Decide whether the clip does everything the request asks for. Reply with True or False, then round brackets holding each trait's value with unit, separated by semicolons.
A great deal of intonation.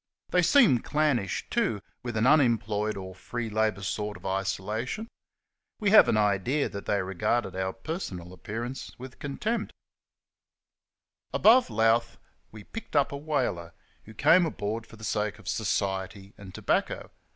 True (5.9 semitones)